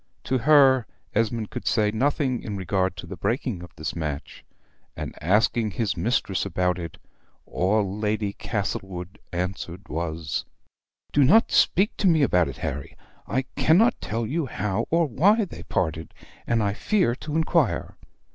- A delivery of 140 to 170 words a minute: Yes, average, 155 wpm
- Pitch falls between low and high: No, low, 105 Hz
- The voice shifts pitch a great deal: Yes, wide, 6.7 semitones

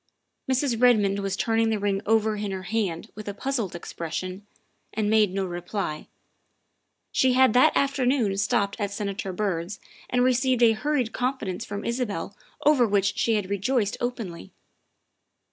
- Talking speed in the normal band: Yes, average, 150 wpm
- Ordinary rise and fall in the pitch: Yes, average, 3.9 semitones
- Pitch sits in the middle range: No, high, 210 Hz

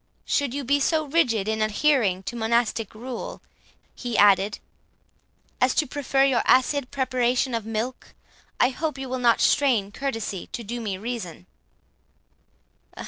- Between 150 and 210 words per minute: No, average, 140 wpm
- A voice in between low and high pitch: No, high, 245 Hz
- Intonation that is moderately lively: Yes, average, 3.7 semitones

